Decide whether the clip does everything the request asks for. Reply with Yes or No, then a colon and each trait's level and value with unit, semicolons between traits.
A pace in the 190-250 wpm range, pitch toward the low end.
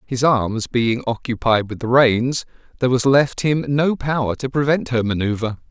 No: average, 180 wpm; low, 125 Hz